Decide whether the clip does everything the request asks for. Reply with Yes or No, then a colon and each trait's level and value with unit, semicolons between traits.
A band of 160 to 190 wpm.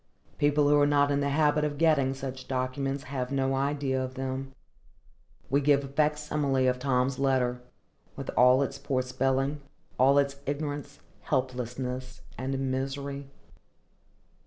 No: average, 140 wpm